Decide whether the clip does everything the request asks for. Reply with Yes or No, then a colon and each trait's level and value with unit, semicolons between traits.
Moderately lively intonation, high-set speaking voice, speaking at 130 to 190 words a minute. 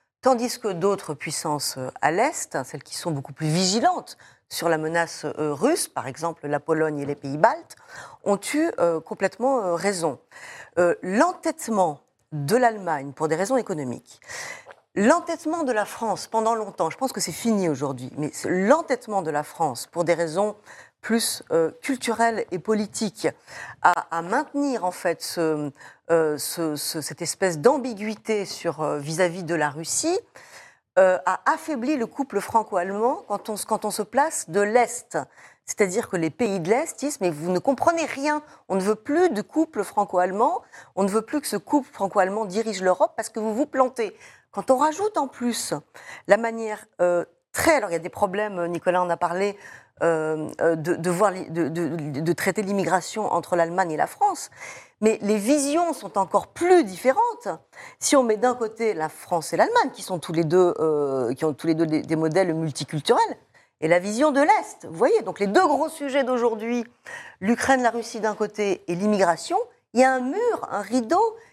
No: wide, 7.0 semitones; high, 205 Hz; average, 185 wpm